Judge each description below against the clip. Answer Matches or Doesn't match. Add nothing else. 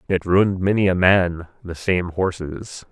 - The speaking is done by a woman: Doesn't match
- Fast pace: Doesn't match